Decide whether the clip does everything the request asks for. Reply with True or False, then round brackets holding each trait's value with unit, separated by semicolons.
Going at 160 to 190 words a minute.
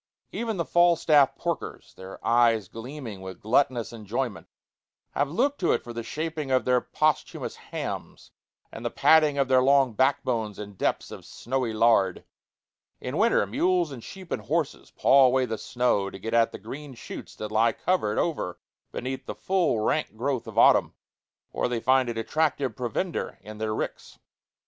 True (170 wpm)